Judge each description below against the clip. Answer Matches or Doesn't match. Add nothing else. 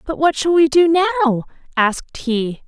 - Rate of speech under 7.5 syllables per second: Matches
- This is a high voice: Matches